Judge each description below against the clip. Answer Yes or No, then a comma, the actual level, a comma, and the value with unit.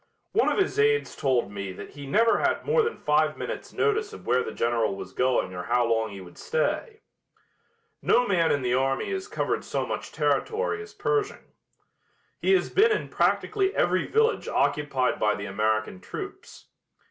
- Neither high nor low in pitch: Yes, medium, 150 Hz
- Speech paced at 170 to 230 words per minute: Yes, average, 180 wpm